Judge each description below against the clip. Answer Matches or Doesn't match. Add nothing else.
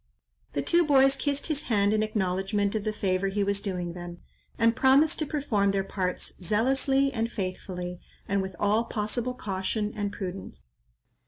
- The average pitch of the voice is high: Matches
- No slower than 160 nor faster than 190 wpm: Matches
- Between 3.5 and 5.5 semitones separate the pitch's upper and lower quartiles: Matches